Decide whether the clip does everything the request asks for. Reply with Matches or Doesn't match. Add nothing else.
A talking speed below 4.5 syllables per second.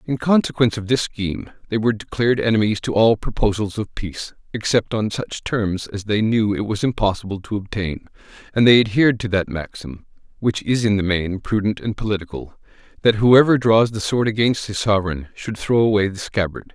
Doesn't match